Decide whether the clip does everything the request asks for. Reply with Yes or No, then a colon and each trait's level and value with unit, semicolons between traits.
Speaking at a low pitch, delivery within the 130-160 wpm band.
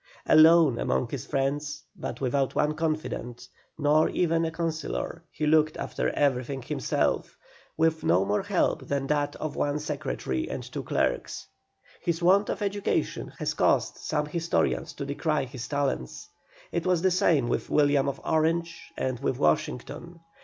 No: medium, 150 Hz; average, 155 wpm